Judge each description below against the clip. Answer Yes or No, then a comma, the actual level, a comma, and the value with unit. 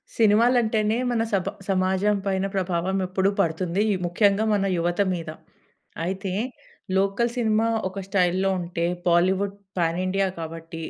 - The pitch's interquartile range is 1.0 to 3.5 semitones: Yes, average, 2.7 semitones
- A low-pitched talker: No, high, 190 Hz